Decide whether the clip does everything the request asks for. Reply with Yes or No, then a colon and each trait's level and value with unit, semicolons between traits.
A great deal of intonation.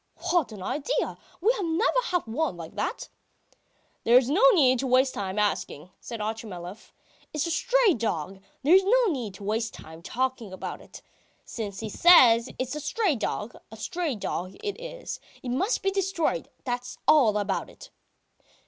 Yes: wide, 8.5 semitones